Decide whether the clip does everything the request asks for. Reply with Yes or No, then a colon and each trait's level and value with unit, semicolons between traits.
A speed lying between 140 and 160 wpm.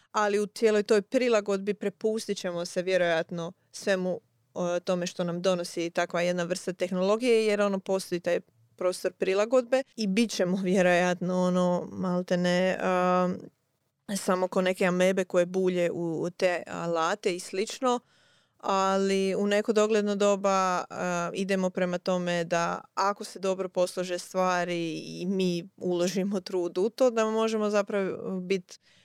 Yes: average, 145 wpm